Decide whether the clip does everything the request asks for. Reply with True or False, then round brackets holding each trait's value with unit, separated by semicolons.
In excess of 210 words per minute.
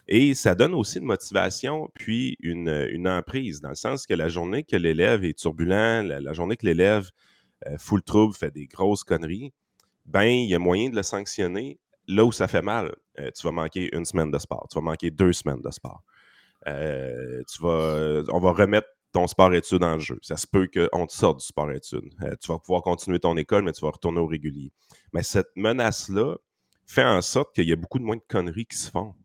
True (220 wpm)